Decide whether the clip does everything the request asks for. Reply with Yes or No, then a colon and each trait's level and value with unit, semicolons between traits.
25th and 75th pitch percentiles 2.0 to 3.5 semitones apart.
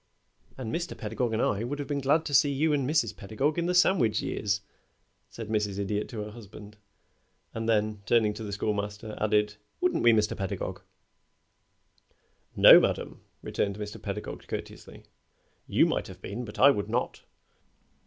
No: average, 4.6 semitones